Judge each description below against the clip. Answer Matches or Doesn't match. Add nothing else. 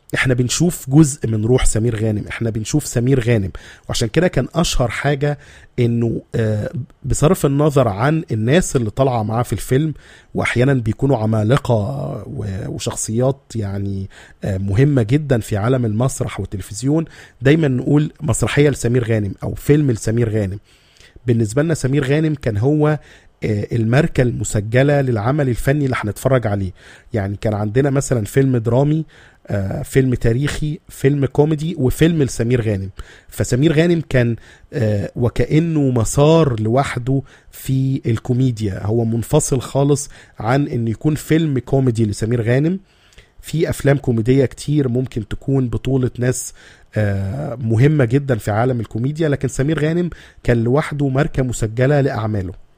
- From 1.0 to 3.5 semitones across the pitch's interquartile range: Doesn't match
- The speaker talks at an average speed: Matches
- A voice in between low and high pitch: Doesn't match